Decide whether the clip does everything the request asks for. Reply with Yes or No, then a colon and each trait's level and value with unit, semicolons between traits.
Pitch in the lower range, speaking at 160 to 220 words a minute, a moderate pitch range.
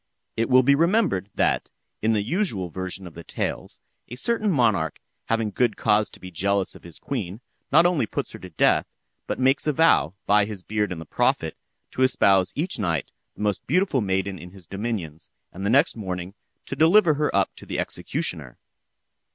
No: low, 105 Hz; average, 190 wpm; wide, 6.8 semitones